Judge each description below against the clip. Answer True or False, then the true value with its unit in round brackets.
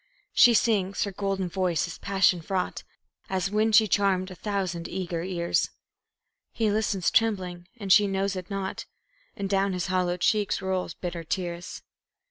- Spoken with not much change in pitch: True (1.8 semitones)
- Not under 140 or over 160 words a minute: True (155 wpm)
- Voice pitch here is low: False (190 Hz)